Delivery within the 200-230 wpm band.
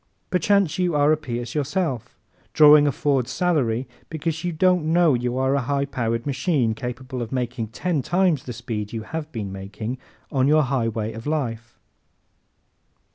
No: average, 165 wpm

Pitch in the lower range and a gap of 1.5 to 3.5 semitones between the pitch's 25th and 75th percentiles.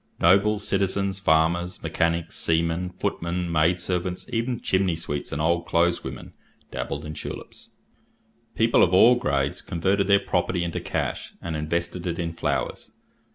Yes: very low, 85 Hz; narrow, 2.4 semitones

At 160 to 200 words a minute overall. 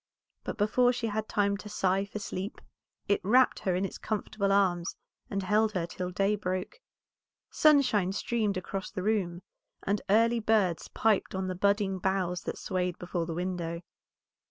Yes: average, 165 wpm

